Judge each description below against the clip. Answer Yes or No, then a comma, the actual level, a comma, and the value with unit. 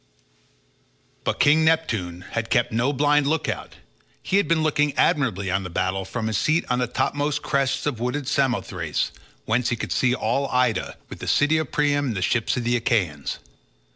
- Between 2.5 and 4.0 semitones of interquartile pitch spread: No, average, 4.9 semitones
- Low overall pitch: Yes, low, 125 Hz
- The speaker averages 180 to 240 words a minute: Yes, average, 190 wpm